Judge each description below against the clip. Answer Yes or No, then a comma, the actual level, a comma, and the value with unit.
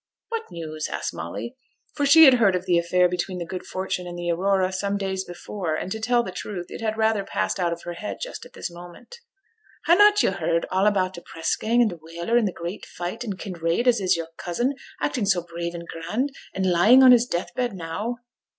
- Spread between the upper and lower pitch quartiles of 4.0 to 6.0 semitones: Yes, average, 4.7 semitones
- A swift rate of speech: Yes, fast, 230 wpm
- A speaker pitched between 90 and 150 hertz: No, high, 190 Hz